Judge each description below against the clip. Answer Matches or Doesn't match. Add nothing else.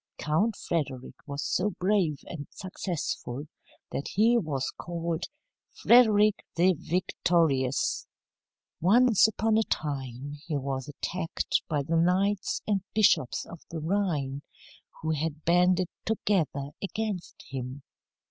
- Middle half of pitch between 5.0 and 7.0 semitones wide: Matches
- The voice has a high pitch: Doesn't match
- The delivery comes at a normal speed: Doesn't match